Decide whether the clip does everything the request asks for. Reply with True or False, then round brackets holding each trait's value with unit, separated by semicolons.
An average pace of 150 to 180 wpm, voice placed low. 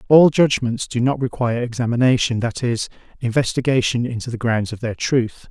True (165 wpm; 120 Hz)